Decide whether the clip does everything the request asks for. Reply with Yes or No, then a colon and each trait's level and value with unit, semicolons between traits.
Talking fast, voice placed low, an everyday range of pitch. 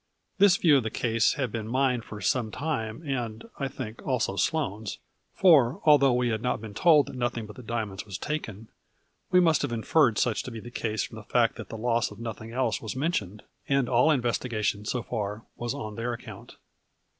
Yes: fast, 210 wpm; low, 120 Hz; average, 3.7 semitones